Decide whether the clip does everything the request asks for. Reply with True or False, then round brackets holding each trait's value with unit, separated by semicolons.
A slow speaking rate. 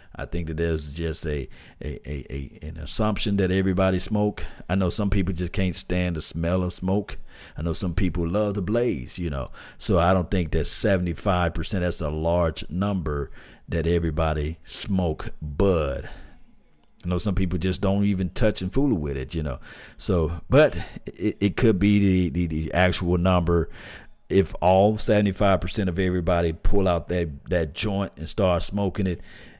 False (175 wpm)